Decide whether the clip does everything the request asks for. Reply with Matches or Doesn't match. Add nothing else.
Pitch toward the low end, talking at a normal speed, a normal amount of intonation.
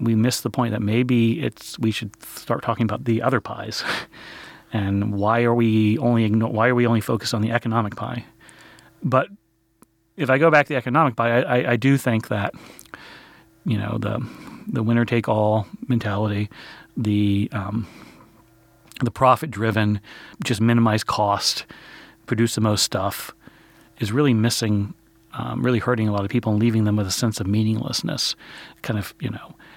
Doesn't match